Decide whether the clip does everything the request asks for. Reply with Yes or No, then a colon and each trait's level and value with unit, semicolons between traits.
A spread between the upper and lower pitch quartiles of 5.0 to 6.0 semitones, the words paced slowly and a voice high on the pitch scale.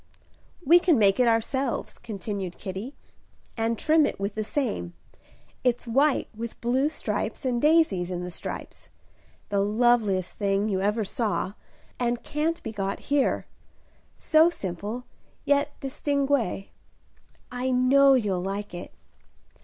Yes: wide, 5.6 semitones; slow, 130 wpm; high, 230 Hz